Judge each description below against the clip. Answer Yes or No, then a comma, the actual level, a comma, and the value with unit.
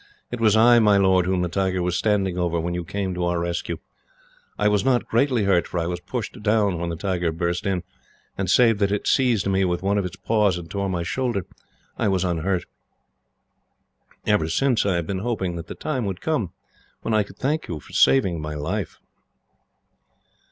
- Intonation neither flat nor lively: Yes, average, 3.6 semitones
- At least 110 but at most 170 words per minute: No, fast, 205 wpm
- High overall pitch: No, very low, 95 Hz